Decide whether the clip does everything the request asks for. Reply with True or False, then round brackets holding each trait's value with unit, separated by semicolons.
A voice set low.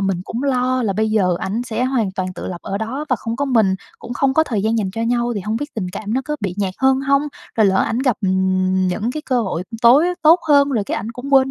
False (230 Hz)